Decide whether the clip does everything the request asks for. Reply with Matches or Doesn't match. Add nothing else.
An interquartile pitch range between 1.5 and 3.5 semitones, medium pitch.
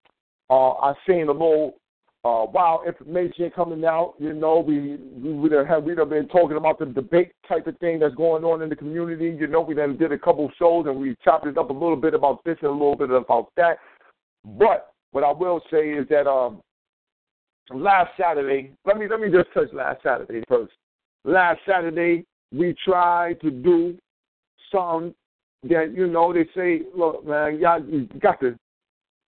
Matches